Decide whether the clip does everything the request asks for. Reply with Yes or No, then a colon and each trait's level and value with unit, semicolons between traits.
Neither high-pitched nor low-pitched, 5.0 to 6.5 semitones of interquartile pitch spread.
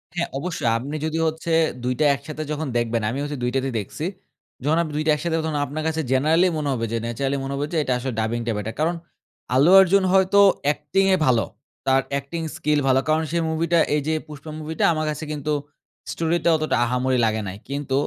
No: medium, 150 Hz; average, 3.4 semitones